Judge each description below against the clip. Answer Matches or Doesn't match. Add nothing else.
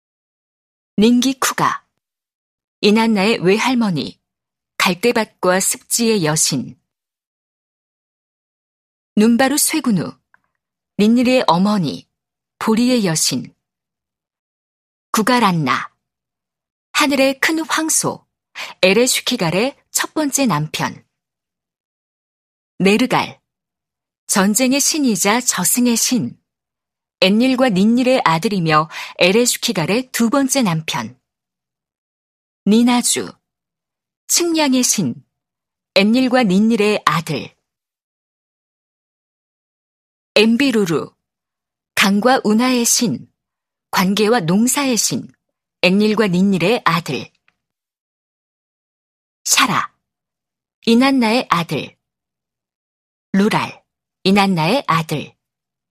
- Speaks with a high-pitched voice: Matches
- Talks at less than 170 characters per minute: Matches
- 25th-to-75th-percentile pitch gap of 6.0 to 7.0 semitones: Doesn't match